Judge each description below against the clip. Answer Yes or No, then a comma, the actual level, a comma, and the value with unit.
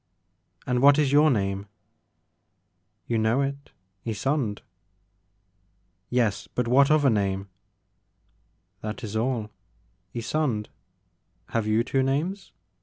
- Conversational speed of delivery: No, slow, 120 wpm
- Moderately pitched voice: No, low, 115 Hz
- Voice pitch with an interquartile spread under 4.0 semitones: No, average, 5.0 semitones